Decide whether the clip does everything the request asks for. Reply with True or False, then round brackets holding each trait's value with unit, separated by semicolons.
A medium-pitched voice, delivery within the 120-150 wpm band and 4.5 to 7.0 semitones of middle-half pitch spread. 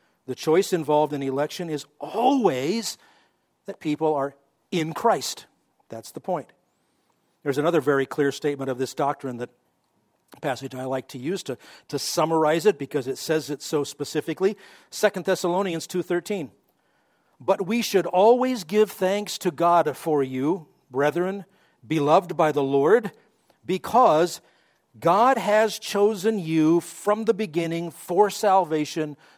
True (165 Hz; 140 wpm; 5.1 semitones)